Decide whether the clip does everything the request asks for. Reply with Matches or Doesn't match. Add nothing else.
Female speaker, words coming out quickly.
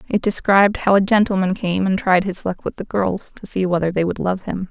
Matches